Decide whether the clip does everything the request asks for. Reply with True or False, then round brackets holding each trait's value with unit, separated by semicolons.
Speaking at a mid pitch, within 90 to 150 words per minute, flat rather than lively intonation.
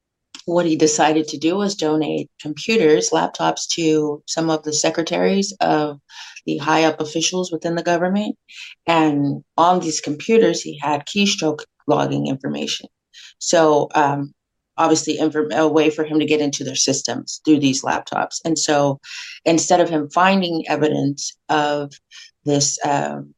True (155 Hz; 145 wpm; 2.1 semitones)